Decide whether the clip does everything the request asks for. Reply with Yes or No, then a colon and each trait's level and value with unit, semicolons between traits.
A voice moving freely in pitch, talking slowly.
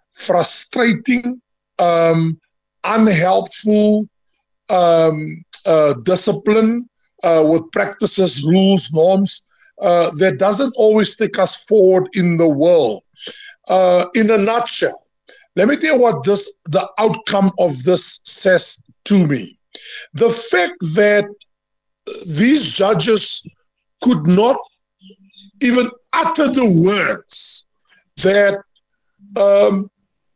No: average, 4.2 semitones; slow, 100 wpm